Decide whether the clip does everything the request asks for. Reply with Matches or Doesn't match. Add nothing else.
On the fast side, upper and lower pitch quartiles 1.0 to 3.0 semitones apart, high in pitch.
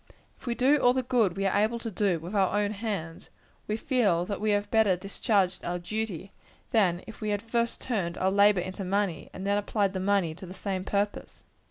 Matches